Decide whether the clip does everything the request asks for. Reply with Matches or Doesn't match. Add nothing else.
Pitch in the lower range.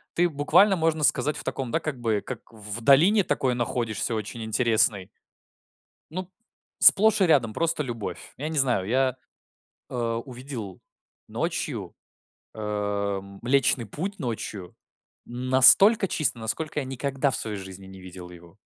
Matches